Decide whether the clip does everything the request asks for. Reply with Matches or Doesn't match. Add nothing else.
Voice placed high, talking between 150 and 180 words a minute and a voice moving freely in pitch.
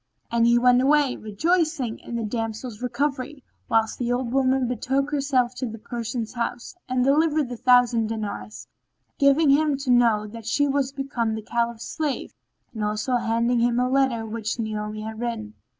Doesn't match